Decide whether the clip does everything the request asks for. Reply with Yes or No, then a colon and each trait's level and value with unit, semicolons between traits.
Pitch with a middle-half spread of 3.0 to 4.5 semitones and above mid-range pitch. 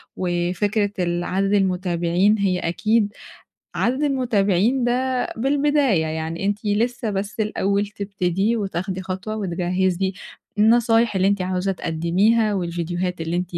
Yes: average, 3.3 semitones; high, 195 Hz